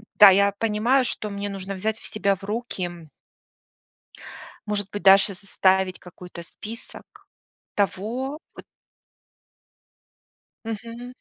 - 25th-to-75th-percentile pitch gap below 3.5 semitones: Yes, average, 2.8 semitones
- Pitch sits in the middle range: No, high, 205 Hz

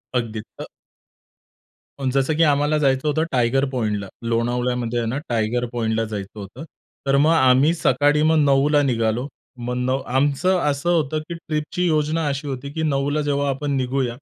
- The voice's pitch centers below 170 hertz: Yes, low, 135 Hz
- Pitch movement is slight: No, average, 3.5 semitones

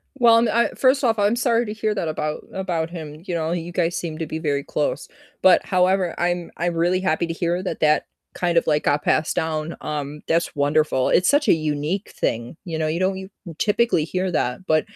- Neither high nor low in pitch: Yes, medium, 170 Hz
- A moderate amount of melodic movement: Yes, average, 3.5 semitones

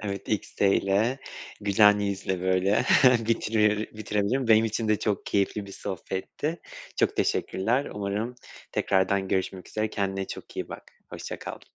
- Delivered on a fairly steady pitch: Yes, narrow, 2.1 semitones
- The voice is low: Yes, low, 105 Hz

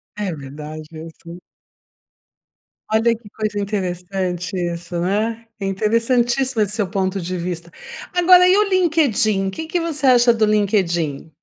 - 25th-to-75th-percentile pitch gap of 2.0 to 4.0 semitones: No, average, 5.1 semitones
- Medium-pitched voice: No, high, 205 Hz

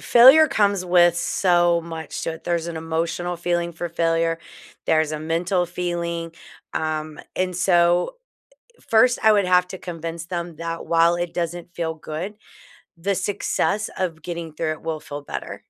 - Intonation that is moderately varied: No, narrow, 1.6 semitones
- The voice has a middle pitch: Yes, medium, 170 Hz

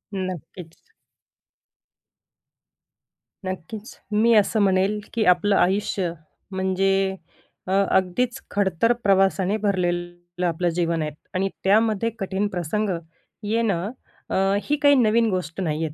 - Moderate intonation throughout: Yes, average, 3.0 semitones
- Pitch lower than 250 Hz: Yes, high, 190 Hz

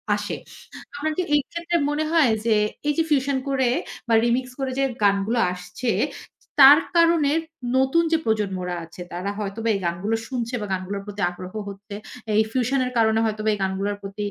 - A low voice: No, high, 225 Hz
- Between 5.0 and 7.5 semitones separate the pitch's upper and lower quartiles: Yes, average, 5.3 semitones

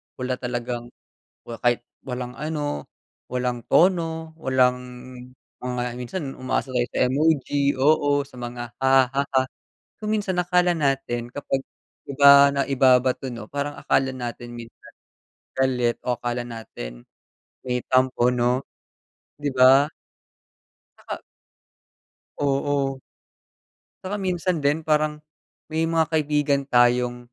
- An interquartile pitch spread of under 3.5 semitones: Yes, average, 3.0 semitones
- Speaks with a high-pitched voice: No, low, 130 Hz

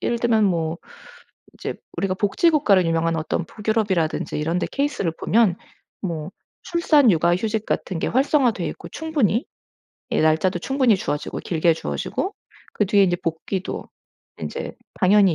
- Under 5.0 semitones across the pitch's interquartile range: No, wide, 5.6 semitones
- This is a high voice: Yes, high, 195 Hz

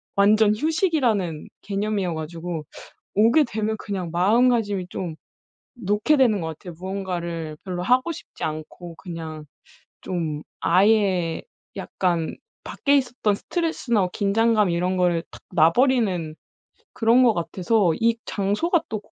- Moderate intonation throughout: Yes, average, 4.8 semitones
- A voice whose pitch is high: Yes, high, 195 Hz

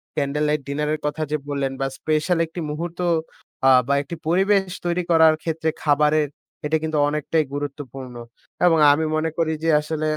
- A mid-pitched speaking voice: Yes, medium, 155 Hz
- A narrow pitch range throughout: Yes, narrow, 1.9 semitones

